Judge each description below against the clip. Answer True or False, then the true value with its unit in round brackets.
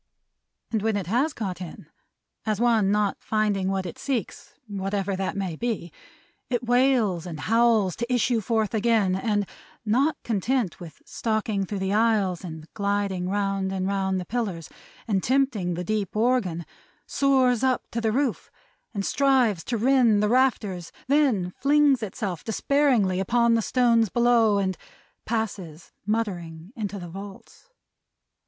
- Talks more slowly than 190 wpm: True (150 wpm)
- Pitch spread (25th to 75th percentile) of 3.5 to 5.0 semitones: True (3.9 semitones)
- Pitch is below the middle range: False (210 Hz)